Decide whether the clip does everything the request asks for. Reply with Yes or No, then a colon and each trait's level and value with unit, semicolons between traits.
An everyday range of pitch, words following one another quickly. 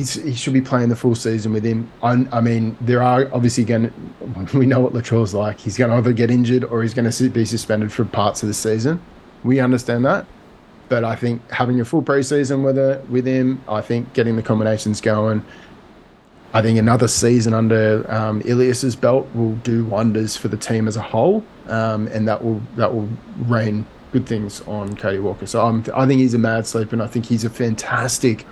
No: narrow, 2.2 semitones; fast, 220 wpm